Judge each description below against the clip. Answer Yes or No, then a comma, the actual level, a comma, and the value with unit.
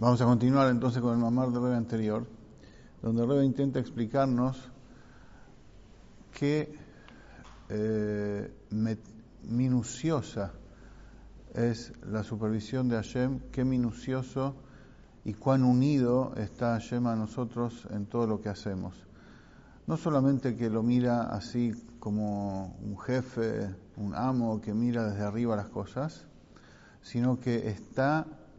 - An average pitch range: Yes, average, 3.0 semitones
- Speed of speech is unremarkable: No, slow, 120 wpm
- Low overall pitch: Yes, low, 120 Hz